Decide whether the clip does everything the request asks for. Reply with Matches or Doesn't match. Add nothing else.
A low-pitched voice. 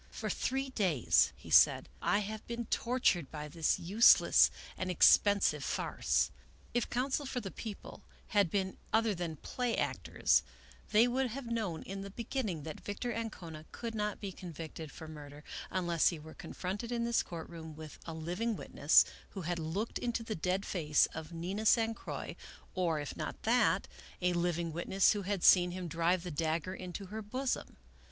Doesn't match